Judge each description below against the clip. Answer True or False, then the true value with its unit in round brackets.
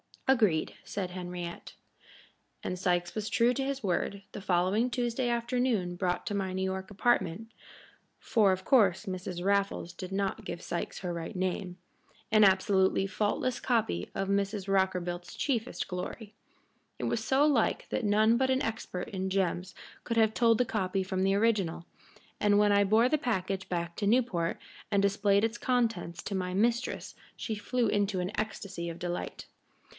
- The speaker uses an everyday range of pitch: True (3.6 semitones)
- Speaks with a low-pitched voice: False (200 Hz)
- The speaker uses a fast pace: False (165 wpm)